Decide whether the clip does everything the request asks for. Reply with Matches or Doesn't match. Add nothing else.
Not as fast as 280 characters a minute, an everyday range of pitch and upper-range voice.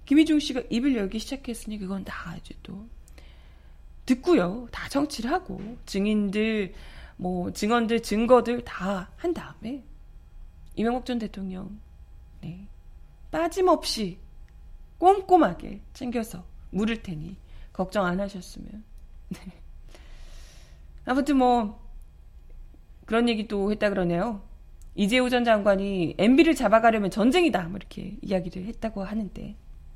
Matches